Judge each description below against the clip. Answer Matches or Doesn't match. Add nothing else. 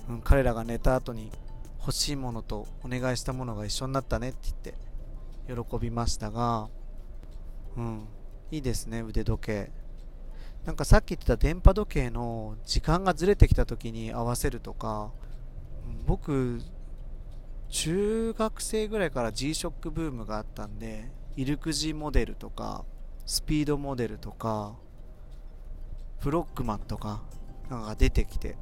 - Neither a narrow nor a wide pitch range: Matches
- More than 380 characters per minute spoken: Doesn't match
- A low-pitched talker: Matches